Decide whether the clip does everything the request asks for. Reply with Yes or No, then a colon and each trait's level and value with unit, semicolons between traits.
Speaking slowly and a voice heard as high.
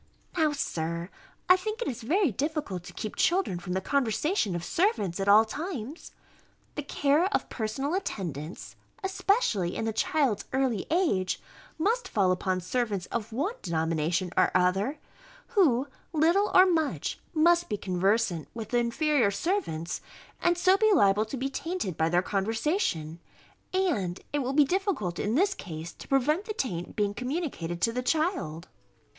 No: average, 160 wpm; high, 240 Hz